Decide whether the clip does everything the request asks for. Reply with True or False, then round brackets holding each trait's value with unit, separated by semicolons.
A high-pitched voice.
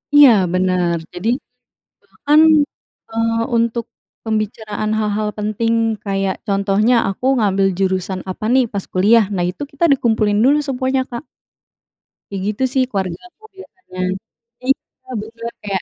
True (215 Hz)